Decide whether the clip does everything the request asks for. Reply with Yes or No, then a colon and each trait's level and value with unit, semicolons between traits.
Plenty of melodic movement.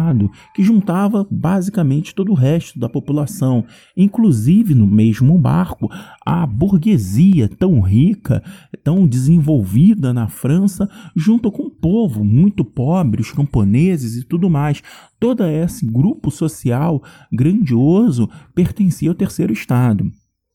Yes: wide, 6.6 semitones